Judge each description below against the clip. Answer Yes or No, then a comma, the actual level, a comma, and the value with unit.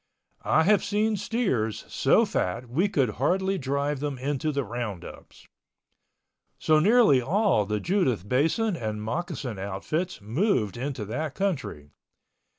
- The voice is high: No, medium, 140 Hz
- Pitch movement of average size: No, wide, 8.7 semitones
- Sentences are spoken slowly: Yes, slow, 130 wpm